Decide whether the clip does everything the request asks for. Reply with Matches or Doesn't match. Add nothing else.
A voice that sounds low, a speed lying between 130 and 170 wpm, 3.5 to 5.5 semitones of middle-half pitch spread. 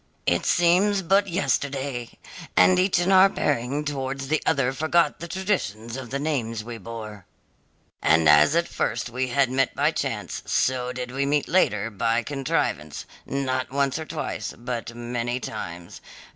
Matches